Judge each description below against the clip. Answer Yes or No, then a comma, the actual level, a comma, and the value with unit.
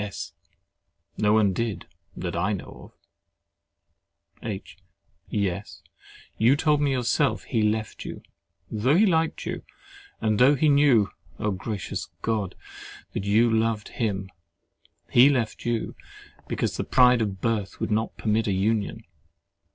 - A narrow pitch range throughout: No, average, 3.3 semitones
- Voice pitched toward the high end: No, low, 110 Hz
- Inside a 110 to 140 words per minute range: Yes, slow, 135 wpm